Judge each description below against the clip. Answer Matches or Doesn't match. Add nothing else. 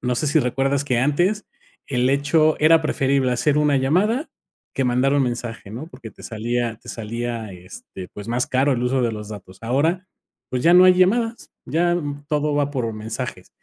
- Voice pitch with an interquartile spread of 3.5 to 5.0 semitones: Matches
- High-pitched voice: Doesn't match